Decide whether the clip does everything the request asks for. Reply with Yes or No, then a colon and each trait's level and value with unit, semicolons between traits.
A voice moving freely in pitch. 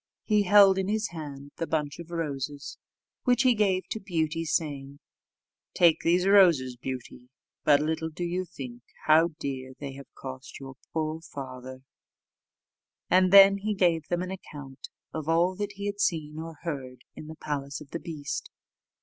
No: average, 4.7 semitones